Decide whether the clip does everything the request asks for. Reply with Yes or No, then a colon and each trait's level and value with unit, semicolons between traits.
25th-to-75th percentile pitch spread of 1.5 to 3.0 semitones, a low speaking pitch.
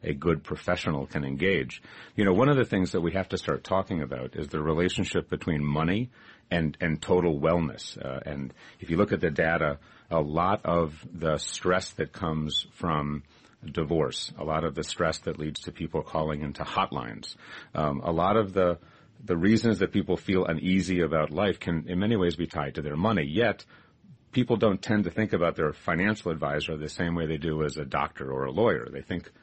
No: average, 3.8 semitones; very low, 85 Hz